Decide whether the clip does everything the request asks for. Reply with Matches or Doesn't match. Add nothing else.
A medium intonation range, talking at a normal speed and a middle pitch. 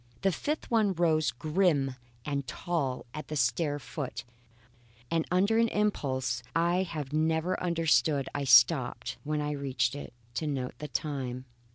Matches